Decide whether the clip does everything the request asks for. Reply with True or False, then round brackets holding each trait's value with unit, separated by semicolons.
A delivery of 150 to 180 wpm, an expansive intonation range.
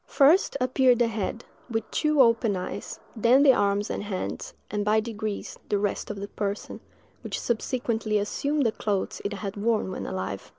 False (175 wpm; 3.1 semitones)